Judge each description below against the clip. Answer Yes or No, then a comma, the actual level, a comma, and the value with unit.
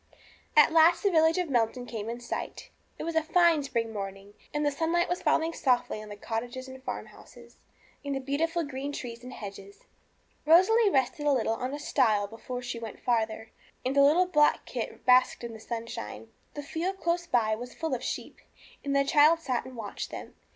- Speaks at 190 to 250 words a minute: Yes, average, 200 wpm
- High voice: Yes, very high, 265 Hz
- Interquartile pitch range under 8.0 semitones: Yes, wide, 5.6 semitones